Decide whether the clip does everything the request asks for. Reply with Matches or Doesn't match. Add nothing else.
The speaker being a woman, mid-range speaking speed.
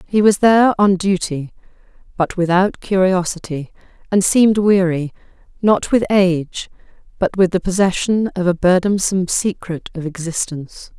Doesn't match